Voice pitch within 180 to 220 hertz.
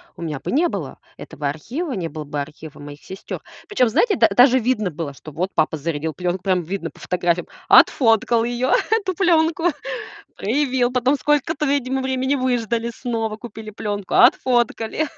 No: high, 230 Hz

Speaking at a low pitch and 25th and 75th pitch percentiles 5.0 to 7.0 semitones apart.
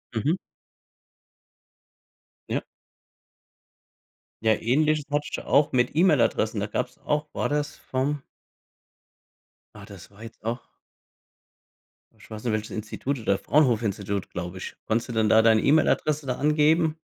Yes: low, 120 Hz; wide, 5.4 semitones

